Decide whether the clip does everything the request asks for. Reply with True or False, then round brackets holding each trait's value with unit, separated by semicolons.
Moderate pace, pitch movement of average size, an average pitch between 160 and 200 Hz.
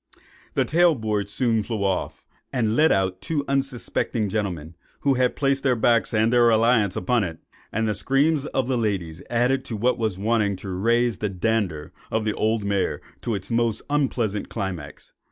False (175 wpm; 3.7 semitones; 110 Hz)